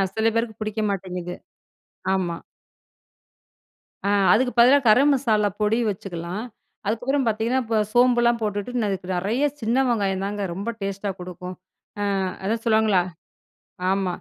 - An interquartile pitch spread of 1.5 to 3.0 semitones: No, average, 3.5 semitones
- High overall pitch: Yes, high, 215 Hz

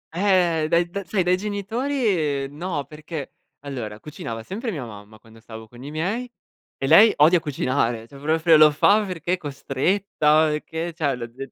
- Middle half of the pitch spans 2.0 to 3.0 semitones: No, average, 5.2 semitones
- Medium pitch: Yes, medium, 155 Hz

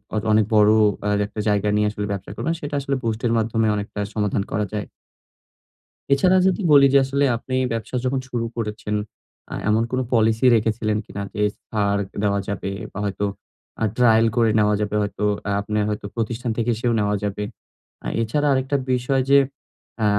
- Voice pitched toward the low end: Yes, low, 110 Hz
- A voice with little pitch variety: No, average, 3.0 semitones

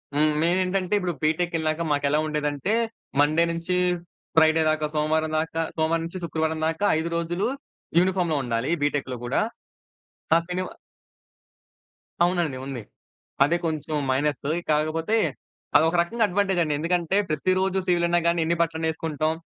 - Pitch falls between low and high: Yes, medium, 160 Hz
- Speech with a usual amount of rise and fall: No, narrow, 2.3 semitones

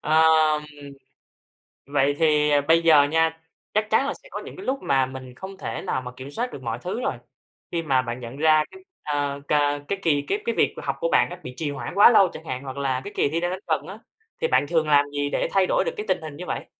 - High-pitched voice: No, medium, 155 Hz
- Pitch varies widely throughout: No, average, 4.8 semitones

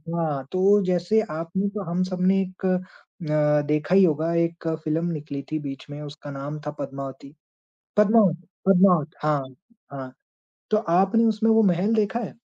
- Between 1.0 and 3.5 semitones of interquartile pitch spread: No, average, 4.4 semitones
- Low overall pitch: No, medium, 175 Hz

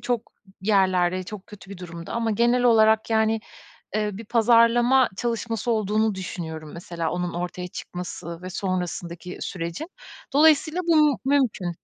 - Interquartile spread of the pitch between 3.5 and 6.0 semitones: Yes, average, 4.7 semitones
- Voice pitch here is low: No, high, 210 Hz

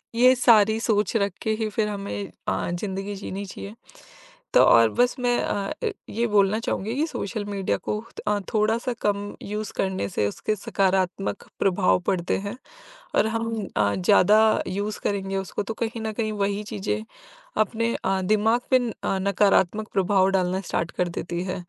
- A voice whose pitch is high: Yes, high, 205 Hz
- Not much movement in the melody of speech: Yes, narrow, 2.3 semitones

